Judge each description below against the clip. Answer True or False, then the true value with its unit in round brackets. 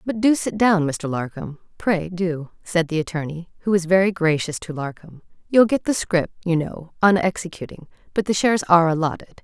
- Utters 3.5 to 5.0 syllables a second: False (5.3 syllables/s)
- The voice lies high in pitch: False (175 Hz)